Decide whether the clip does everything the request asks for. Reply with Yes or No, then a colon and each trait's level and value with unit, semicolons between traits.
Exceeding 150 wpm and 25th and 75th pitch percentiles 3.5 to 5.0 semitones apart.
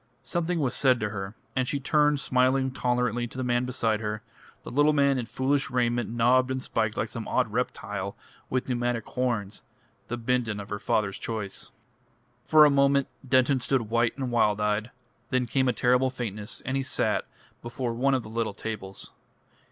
No: average, 185 wpm; average, 2.9 semitones